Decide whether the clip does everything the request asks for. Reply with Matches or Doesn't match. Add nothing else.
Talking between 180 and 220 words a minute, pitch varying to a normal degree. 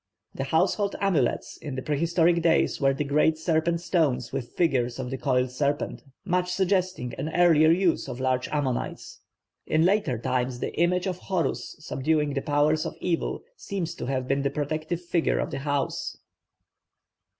Doesn't match